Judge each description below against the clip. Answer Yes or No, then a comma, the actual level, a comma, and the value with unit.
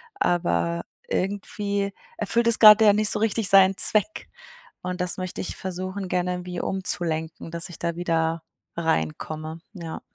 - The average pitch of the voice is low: No, medium, 180 Hz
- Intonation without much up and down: No, average, 3.2 semitones